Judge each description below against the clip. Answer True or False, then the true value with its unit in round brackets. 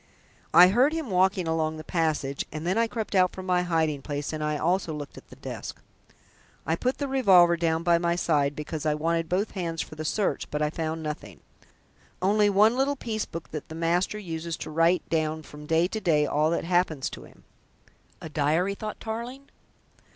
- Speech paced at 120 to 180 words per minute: False (200 wpm)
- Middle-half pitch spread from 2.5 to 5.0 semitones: True (3.7 semitones)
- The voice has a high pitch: False (170 Hz)